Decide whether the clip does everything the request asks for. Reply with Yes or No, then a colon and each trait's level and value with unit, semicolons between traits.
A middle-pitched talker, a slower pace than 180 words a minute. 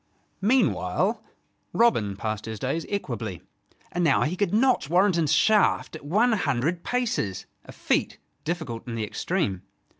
Yes: medium, 165 Hz; average, 140 wpm